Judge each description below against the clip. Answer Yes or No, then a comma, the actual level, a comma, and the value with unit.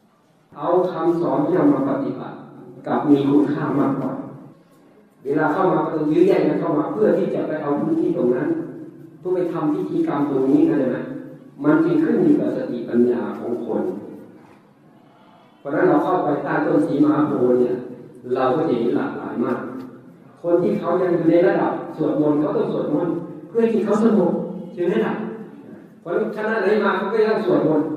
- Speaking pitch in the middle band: Yes, medium, 175 Hz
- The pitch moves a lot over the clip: Yes, wide, 6.1 semitones